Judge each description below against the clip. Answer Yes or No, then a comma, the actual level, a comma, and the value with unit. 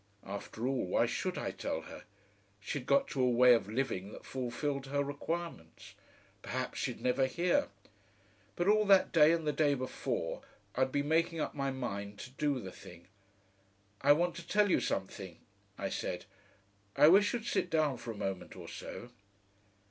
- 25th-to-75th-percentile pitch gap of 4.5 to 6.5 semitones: Yes, wide, 5.4 semitones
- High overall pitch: No, low, 135 Hz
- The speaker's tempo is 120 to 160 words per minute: No, average, 175 wpm